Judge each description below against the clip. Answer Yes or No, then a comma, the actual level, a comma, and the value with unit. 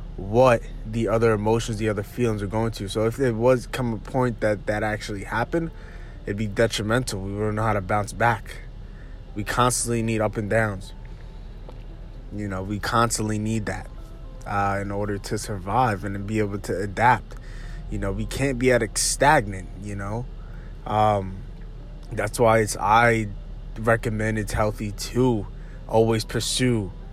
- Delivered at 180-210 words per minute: No, average, 165 wpm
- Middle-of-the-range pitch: No, low, 110 Hz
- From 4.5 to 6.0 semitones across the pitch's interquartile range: No, narrow, 2.5 semitones